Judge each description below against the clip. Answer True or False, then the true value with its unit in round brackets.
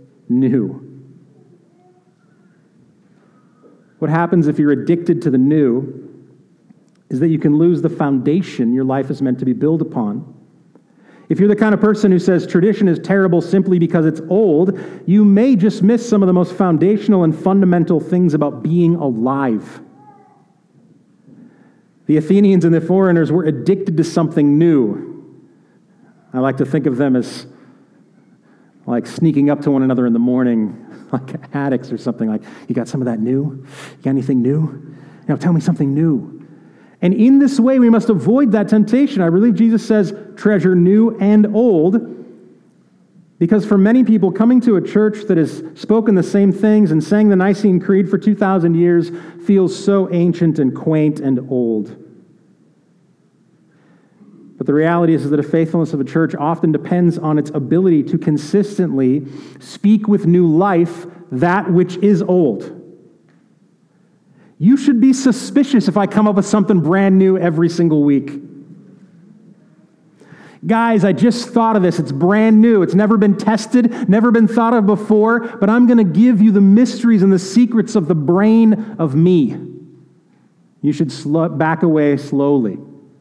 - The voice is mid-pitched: True (180 Hz)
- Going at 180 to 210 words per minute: False (165 wpm)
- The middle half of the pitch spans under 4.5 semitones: False (5.2 semitones)